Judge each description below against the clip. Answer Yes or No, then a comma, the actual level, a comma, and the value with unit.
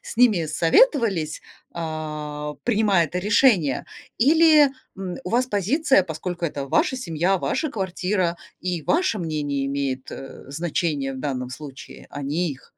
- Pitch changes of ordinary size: No, wide, 6.0 semitones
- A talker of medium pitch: Yes, medium, 170 Hz